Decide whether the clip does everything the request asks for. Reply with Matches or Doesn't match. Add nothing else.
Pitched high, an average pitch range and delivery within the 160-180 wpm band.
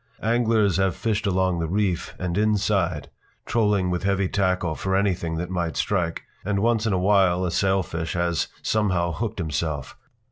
Doesn't match